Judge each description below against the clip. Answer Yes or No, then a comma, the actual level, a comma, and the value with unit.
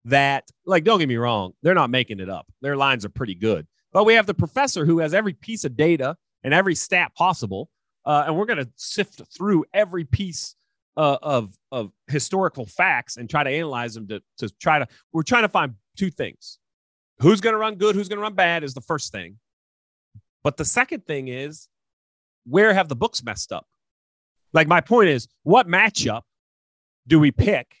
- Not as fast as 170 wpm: No, fast, 205 wpm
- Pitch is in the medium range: Yes, medium, 145 Hz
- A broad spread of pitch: Yes, wide, 8.6 semitones